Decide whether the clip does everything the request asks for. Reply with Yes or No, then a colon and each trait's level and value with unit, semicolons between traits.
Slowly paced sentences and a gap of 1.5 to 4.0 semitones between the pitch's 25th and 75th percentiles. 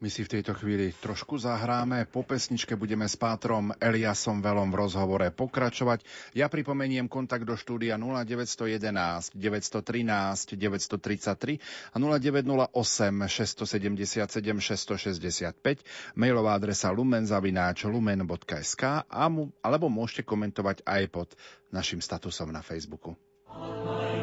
Yes: slow, 105 wpm; average, 3.4 semitones